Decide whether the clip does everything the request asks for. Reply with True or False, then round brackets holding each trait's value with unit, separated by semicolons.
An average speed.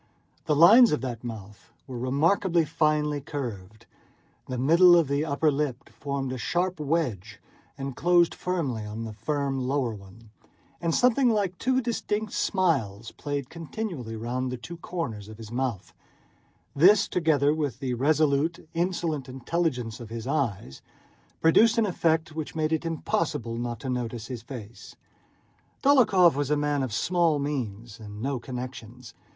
True (150 wpm)